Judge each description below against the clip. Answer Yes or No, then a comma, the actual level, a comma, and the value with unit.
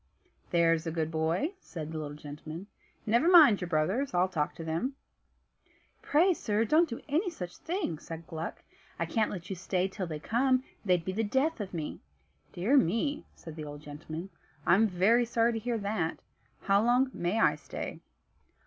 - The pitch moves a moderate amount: No, wide, 6.6 semitones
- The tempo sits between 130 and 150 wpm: No, average, 180 wpm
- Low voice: No, high, 190 Hz